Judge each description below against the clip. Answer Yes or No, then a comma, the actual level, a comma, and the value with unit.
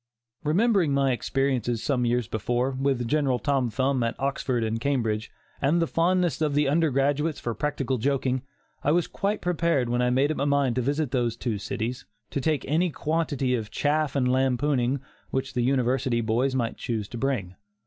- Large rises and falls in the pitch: No, average, 3.1 semitones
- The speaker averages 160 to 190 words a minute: Yes, average, 180 wpm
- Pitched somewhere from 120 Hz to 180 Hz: Yes, low, 135 Hz